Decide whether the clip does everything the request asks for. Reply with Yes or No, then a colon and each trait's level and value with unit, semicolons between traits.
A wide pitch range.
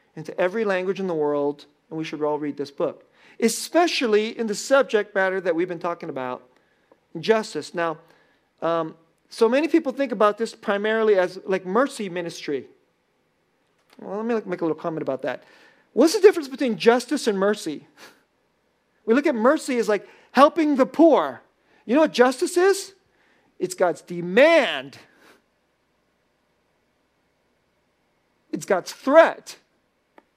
Yes: wide, 7.6 semitones